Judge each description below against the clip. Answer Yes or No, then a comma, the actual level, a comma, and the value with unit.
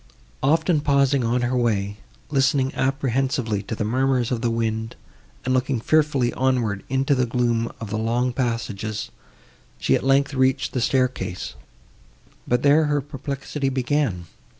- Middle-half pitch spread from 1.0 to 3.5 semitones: Yes, average, 2.9 semitones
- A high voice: No, low, 130 Hz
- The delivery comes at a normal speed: Yes, average, 145 wpm